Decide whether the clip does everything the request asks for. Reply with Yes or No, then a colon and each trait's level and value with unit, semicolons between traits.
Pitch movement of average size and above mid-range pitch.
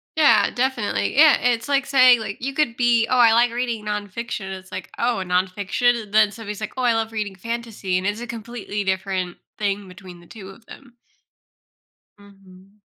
Yes: average, 3.6 semitones; high, 220 Hz